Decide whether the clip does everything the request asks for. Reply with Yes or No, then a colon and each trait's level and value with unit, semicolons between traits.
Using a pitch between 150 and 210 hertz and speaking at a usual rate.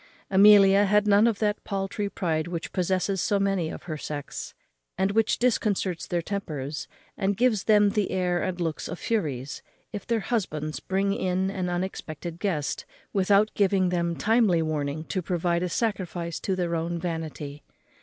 Yes: medium, 185 Hz; average, 165 wpm